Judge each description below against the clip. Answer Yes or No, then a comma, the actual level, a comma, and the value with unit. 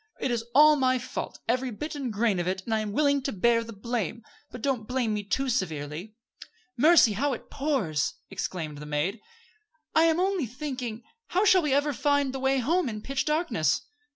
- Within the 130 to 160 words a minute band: No, average, 200 wpm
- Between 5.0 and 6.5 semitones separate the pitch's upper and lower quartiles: Yes, average, 5.3 semitones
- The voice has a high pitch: Yes, high, 245 Hz